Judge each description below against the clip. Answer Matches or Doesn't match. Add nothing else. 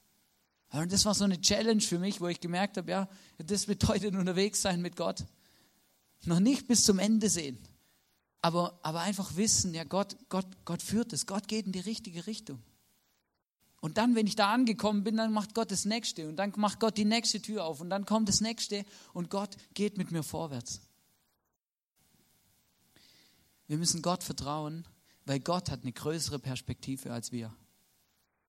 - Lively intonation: Doesn't match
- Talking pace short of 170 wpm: Doesn't match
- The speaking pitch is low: Doesn't match